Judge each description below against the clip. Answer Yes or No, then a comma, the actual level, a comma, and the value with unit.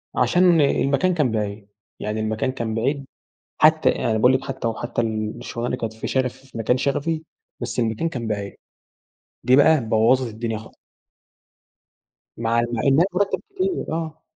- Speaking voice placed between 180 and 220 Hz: No, low, 125 Hz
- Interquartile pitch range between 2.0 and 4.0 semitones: No, average, 4.6 semitones